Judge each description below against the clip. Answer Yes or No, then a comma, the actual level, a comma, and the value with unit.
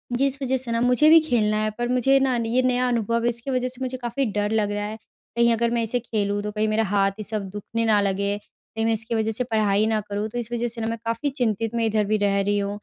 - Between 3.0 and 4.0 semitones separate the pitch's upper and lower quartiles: No, narrow, 2.6 semitones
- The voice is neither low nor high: No, high, 225 Hz